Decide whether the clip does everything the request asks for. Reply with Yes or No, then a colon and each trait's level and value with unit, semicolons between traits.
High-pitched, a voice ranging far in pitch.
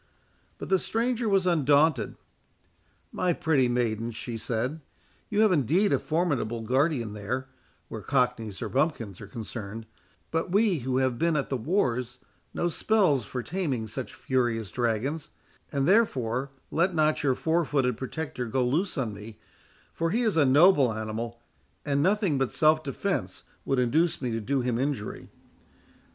No: low, 135 Hz; wide, 5.7 semitones